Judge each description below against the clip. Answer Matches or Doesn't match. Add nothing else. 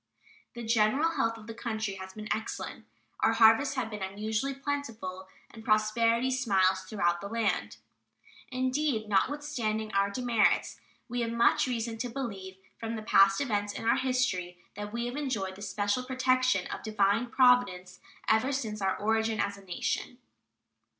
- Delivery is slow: Doesn't match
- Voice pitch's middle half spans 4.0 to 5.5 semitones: Doesn't match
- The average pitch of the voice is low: Doesn't match